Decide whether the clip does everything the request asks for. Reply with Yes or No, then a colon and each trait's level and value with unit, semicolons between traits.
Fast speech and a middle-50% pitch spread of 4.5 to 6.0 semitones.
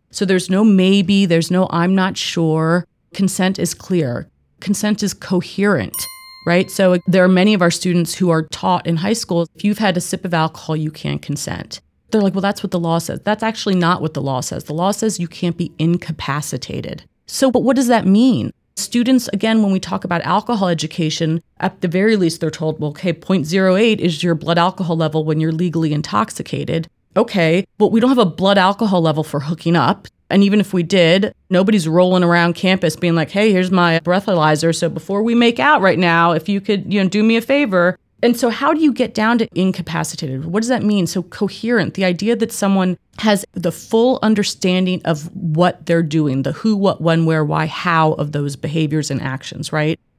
No: fast, 210 wpm; average, 3.6 semitones